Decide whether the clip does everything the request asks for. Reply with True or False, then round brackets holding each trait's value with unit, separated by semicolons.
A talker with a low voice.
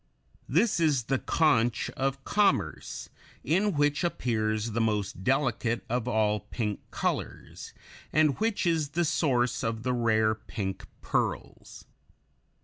True (125 Hz)